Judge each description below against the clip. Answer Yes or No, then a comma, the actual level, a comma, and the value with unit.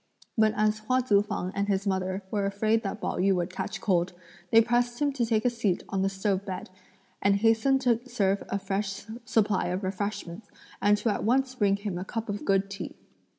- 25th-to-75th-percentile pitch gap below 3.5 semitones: Yes, narrow, 2.6 semitones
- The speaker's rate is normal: No, fast, 215 wpm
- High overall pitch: Yes, high, 205 Hz